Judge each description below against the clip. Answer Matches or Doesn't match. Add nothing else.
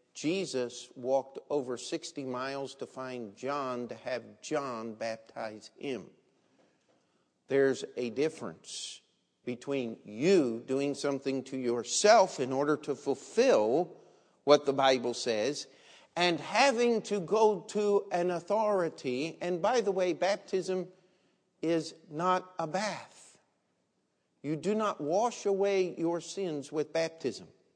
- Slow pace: Matches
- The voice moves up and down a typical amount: Doesn't match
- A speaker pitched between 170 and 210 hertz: Doesn't match